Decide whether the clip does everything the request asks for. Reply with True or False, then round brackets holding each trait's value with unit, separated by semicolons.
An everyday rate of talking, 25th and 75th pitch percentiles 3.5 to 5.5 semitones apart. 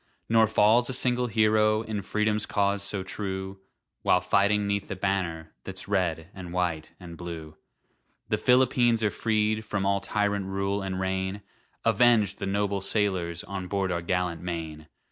False (160 wpm; 2.7 semitones)